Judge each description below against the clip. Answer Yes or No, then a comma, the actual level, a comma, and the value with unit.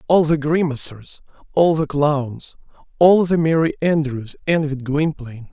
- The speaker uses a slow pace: Yes, slow, 130 wpm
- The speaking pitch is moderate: Yes, medium, 150 Hz